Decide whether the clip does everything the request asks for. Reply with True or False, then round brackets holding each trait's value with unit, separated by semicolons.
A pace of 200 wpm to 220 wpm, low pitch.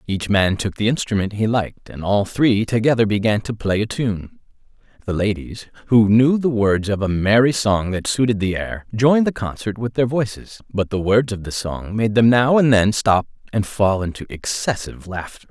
True (205 wpm; 110 Hz)